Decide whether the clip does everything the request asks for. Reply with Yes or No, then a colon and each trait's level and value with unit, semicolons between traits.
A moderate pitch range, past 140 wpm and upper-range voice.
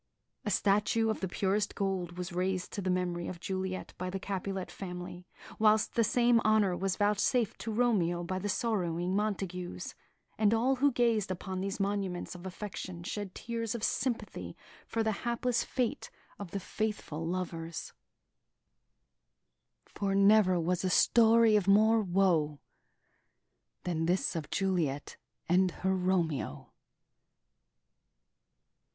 No: average, 3.3 semitones; slow, 135 wpm; high, 195 Hz